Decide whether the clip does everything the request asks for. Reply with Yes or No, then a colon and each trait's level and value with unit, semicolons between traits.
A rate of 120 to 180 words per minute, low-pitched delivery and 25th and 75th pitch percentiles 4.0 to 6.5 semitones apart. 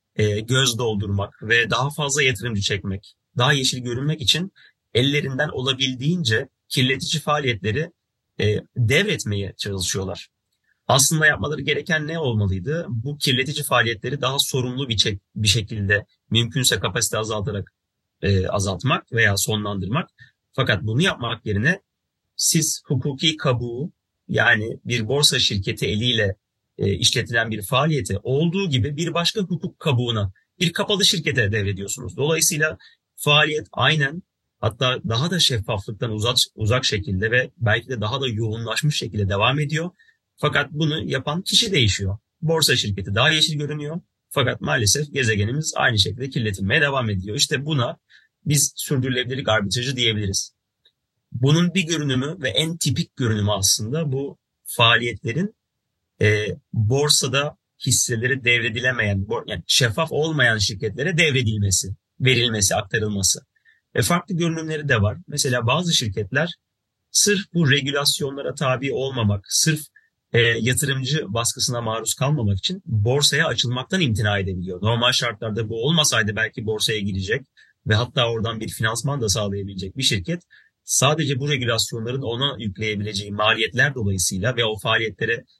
Yes: average, 125 wpm; low, 125 Hz; wide, 5.4 semitones